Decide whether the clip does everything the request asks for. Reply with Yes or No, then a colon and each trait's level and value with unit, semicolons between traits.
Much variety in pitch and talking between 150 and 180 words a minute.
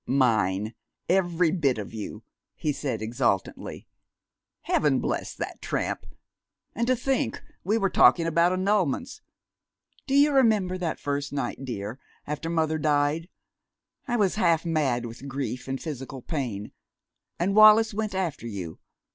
No: wide, 6.8 semitones; average, 140 wpm